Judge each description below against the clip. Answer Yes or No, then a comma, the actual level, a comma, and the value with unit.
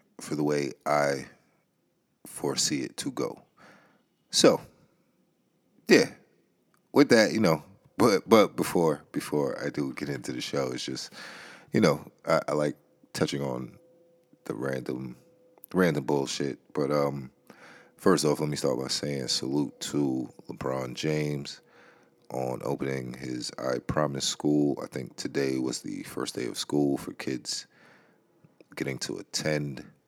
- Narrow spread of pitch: Yes, narrow, 2.2 semitones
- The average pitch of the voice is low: Yes, very low, 70 Hz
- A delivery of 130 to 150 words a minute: Yes, average, 140 wpm